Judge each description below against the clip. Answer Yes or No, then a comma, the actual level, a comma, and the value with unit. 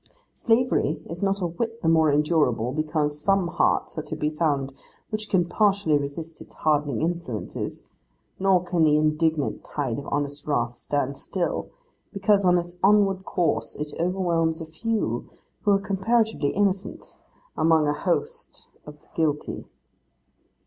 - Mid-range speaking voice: Yes, medium, 165 Hz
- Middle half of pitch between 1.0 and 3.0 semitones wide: No, average, 4.5 semitones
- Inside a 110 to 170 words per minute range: Yes, average, 145 wpm